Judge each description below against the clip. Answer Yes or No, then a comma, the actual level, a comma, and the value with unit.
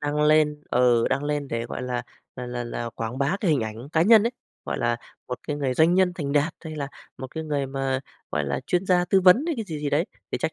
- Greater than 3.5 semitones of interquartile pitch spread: Yes, average, 4.4 semitones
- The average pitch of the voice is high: No, medium, 145 Hz